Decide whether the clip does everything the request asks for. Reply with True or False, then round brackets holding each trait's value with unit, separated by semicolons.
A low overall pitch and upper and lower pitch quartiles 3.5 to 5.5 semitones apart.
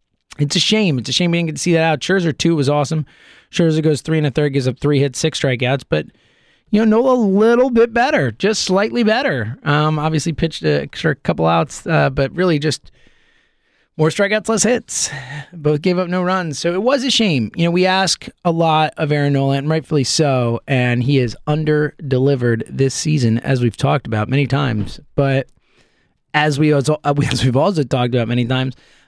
False (150 Hz; 4.3 semitones)